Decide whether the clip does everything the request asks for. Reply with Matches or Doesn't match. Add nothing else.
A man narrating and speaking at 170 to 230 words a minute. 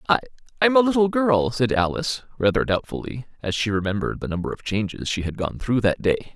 Matches